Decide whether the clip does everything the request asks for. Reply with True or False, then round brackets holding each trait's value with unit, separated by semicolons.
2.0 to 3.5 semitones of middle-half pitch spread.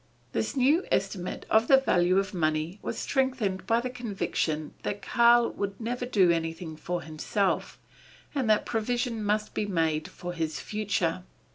False (5.4 semitones)